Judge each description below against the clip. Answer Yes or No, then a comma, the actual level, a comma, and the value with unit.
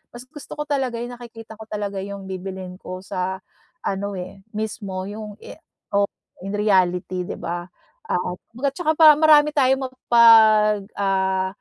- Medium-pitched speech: No, high, 205 Hz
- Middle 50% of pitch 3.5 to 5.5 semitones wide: Yes, average, 4.2 semitones